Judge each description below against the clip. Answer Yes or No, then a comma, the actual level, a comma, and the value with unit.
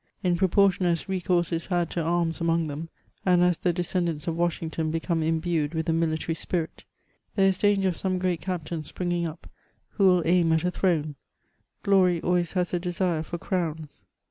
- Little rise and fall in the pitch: Yes, narrow, 1.8 semitones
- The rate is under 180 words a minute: No, average, 190 wpm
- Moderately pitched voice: Yes, medium, 175 Hz